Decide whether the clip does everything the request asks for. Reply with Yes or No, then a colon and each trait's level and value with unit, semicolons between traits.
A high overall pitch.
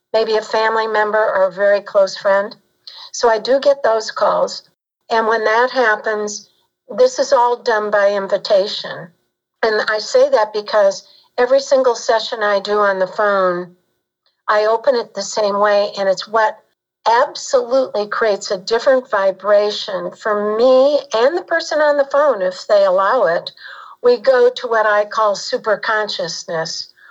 Yes: high, 220 Hz